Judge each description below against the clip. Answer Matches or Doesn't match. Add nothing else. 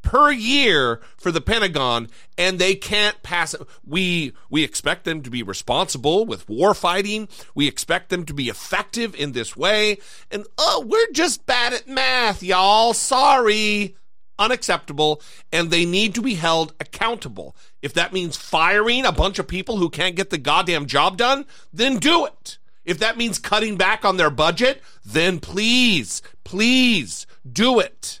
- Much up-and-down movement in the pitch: Matches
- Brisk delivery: Doesn't match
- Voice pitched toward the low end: Doesn't match